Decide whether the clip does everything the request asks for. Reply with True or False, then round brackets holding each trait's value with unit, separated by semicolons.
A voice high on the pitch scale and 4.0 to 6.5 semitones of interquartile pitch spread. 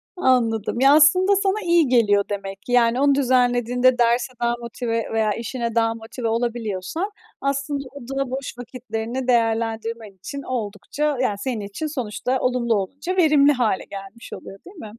False (245 Hz; 3.5 semitones)